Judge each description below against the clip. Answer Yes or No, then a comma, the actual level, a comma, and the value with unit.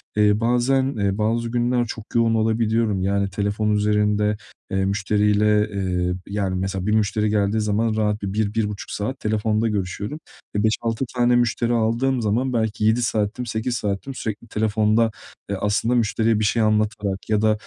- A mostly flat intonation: Yes, narrow, 1.8 semitones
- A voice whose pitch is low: Yes, low, 110 Hz